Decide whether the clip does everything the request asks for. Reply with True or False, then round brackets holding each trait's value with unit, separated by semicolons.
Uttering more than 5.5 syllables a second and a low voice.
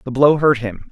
True (5.7 syllables/s; 130 Hz)